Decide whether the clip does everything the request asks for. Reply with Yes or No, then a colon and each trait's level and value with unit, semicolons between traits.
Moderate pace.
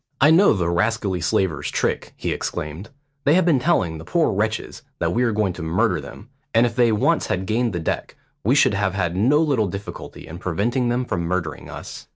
No: fast, 210 wpm